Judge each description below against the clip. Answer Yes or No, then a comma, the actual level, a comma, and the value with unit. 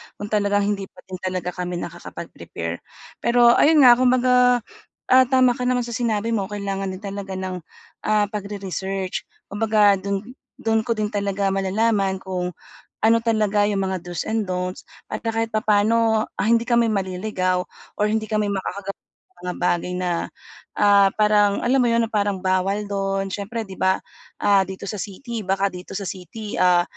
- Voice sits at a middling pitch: No, high, 205 Hz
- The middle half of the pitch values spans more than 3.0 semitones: No, average, 2.7 semitones